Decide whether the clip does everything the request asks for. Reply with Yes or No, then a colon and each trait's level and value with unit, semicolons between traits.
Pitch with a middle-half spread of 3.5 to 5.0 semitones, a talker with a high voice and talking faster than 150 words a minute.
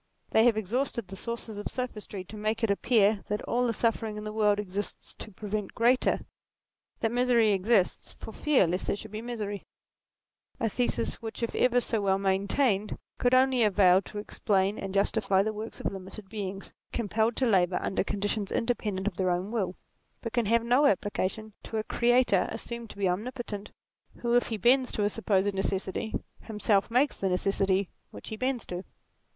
No: average, 3.1 semitones; high, 210 Hz; average, 190 wpm